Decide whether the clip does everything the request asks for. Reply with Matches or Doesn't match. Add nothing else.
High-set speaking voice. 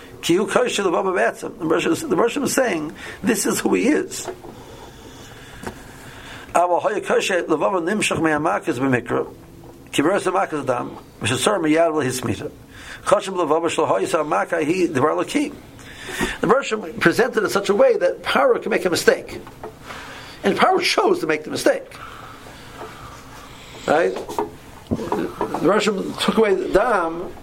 Matches